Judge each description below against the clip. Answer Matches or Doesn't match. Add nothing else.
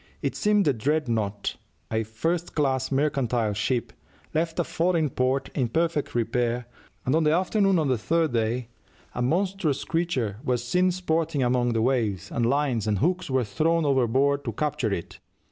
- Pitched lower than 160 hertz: Matches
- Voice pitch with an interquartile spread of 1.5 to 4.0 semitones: Doesn't match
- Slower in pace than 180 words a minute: Matches